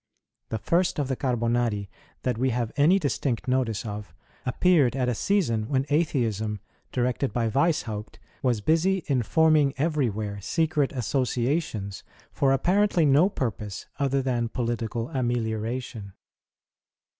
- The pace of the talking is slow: Yes, slow, 125 wpm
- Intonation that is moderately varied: Yes, average, 4.5 semitones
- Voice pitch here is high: No, low, 125 Hz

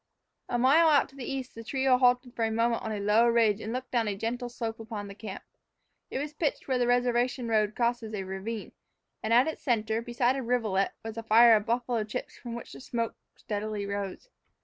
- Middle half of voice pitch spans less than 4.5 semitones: Yes, narrow, 2.4 semitones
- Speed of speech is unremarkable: No, fast, 220 wpm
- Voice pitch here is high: Yes, high, 235 Hz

